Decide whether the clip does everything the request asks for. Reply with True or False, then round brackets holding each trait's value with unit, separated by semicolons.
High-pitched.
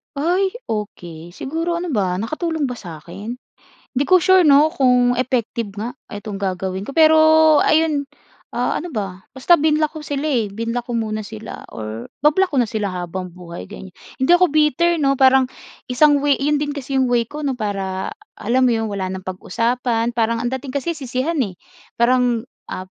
True (245 Hz)